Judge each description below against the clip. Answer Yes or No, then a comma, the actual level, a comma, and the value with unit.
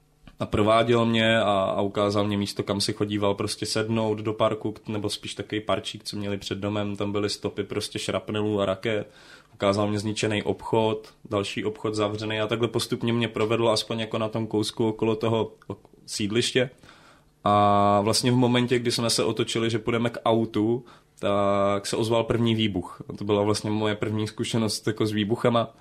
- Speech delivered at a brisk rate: Yes, fast, 175 wpm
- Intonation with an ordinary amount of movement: No, narrow, 1.9 semitones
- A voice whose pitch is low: Yes, low, 110 Hz